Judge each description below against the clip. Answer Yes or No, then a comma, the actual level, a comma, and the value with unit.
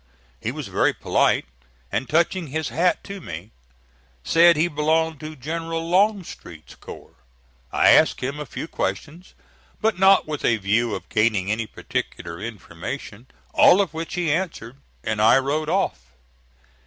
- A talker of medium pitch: Yes, medium, 150 Hz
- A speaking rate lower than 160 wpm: Yes, average, 150 wpm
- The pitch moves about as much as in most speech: No, wide, 6.7 semitones